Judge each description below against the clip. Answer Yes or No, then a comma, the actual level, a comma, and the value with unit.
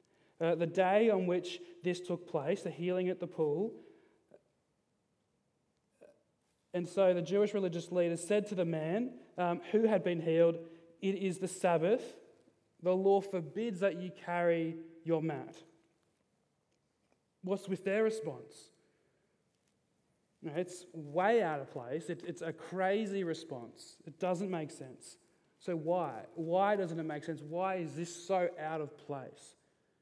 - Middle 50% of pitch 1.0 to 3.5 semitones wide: Yes, average, 2.7 semitones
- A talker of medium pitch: Yes, medium, 180 Hz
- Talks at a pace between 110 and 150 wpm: Yes, average, 145 wpm